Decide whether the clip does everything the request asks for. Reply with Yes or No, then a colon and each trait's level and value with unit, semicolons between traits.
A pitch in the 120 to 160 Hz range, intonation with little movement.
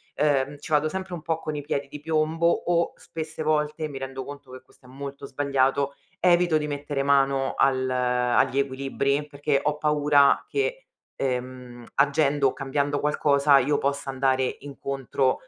Yes: medium, 140 Hz; narrow, 1.9 semitones